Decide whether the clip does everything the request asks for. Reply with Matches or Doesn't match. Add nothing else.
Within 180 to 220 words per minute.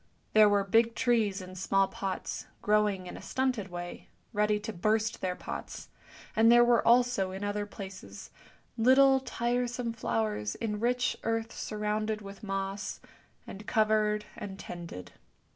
Doesn't match